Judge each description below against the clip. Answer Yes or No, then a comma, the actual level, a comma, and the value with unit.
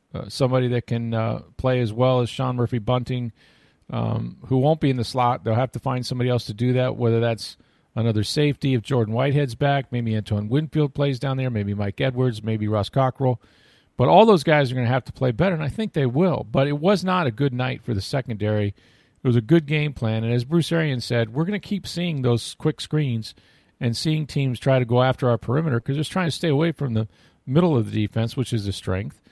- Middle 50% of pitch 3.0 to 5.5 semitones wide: Yes, average, 3.7 semitones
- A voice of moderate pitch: No, low, 125 Hz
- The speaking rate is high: Yes, fast, 240 wpm